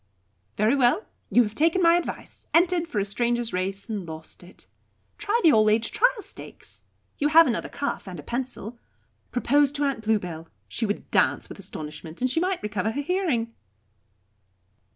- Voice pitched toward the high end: Yes, high, 240 Hz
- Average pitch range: No, wide, 7.5 semitones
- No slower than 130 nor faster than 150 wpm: No, average, 175 wpm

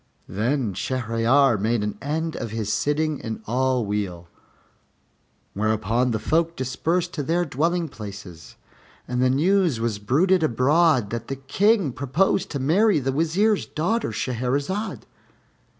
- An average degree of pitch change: No, wide, 6.4 semitones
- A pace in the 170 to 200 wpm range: No, slow, 135 wpm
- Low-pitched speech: Yes, low, 130 Hz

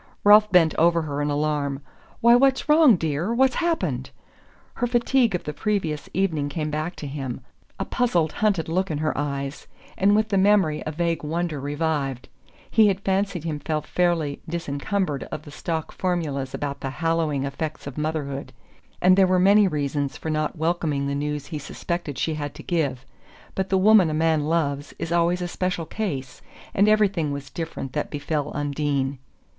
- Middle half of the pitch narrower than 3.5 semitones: No, average, 4.4 semitones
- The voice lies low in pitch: No, medium, 160 Hz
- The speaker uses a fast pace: No, average, 175 wpm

